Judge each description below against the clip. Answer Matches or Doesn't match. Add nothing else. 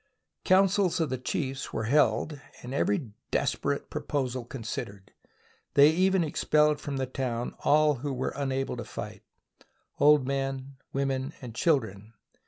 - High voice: Doesn't match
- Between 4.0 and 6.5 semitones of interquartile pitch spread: Doesn't match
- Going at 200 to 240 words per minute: Doesn't match